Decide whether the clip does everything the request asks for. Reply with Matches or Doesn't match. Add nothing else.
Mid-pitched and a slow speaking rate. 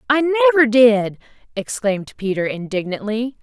Doesn't match